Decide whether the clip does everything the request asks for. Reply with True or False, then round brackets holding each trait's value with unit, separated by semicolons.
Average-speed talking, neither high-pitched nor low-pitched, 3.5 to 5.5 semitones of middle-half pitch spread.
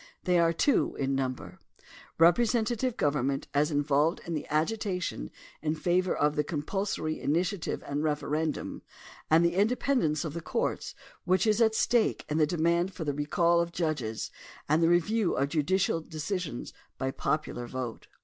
True (160 wpm; 165 Hz; 3.8 semitones)